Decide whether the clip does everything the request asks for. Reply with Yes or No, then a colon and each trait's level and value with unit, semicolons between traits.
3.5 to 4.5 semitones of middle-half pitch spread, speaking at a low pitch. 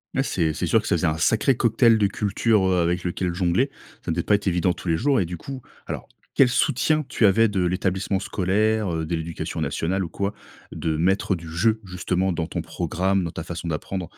Yes: average, 3.9 semitones; very low, 95 Hz